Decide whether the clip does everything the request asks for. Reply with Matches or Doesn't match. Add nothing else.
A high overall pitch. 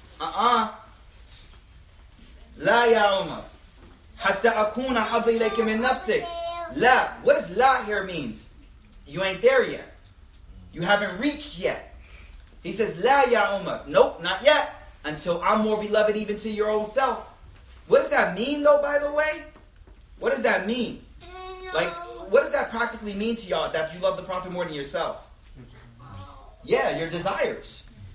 Matches